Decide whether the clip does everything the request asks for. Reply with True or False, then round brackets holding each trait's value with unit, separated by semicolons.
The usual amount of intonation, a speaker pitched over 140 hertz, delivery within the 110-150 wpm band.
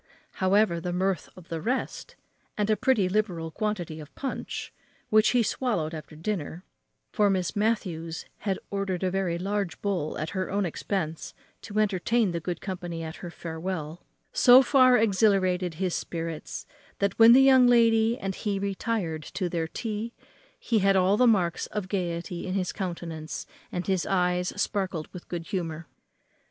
False (3.7 semitones; 190 Hz; 165 wpm)